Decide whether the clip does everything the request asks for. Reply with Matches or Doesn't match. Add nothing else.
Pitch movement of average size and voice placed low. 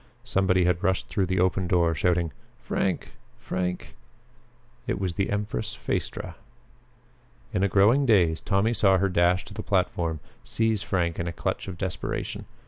Doesn't match